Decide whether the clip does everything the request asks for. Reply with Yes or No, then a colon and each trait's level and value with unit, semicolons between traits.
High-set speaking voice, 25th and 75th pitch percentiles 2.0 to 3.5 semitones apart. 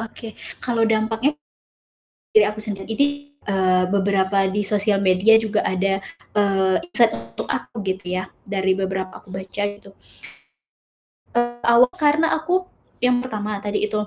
Yes: high, 205 Hz; average, 2.9 semitones